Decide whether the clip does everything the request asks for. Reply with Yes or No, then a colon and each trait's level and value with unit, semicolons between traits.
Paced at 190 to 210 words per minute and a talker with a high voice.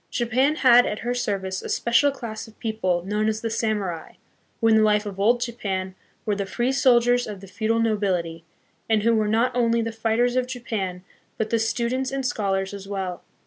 Yes: average, 200 wpm; high, 220 Hz